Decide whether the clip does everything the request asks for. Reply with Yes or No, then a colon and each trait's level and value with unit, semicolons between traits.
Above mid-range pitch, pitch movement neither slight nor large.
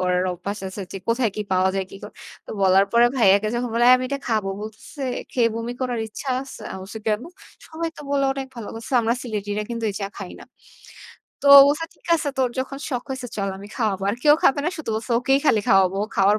Yes: high, 225 Hz; average, 4.6 semitones